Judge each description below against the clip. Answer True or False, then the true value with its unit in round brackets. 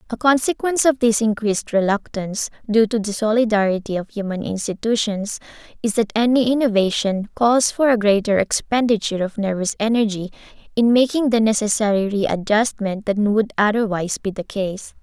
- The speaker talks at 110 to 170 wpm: True (145 wpm)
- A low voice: False (215 Hz)